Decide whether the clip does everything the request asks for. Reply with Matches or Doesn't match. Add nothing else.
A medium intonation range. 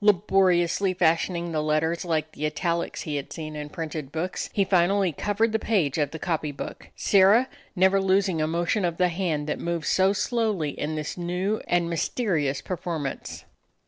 Matches